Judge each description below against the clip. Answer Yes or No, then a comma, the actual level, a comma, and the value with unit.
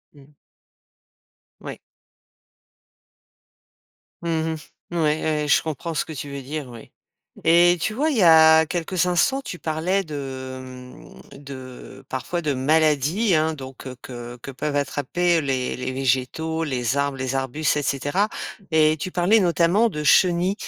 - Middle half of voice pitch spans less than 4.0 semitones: No, average, 4.3 semitones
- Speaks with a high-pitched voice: No, medium, 155 Hz